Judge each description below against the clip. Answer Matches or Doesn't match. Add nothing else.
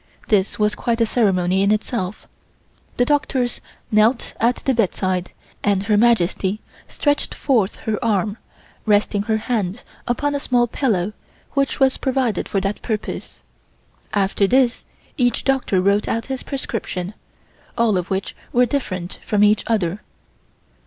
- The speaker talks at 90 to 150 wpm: Matches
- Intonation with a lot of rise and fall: Doesn't match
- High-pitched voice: Matches